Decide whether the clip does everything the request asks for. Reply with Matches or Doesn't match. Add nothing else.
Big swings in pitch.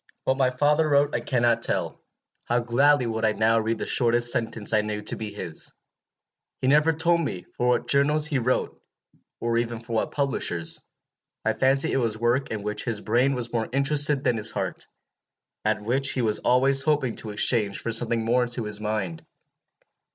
Doesn't match